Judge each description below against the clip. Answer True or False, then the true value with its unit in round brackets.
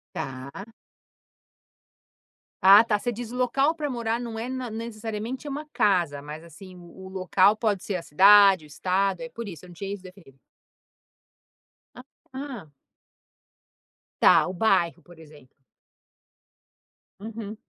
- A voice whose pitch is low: False (200 Hz)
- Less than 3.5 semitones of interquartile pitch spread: False (4.7 semitones)